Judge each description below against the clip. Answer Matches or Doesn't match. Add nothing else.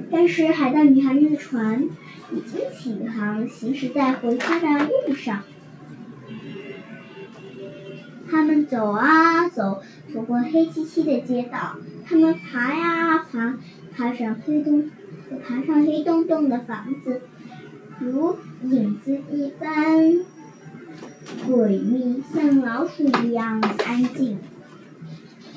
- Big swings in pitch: Doesn't match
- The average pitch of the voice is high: Matches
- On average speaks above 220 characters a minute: Doesn't match